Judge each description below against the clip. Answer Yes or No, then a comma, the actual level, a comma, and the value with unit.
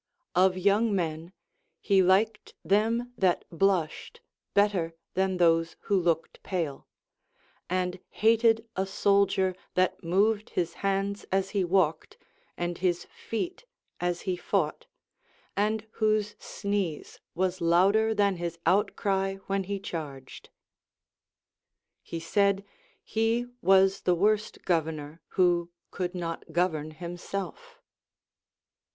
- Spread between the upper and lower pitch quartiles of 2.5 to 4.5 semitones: Yes, average, 2.8 semitones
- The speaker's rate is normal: No, slow, 110 wpm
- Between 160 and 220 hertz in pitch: Yes, high, 190 Hz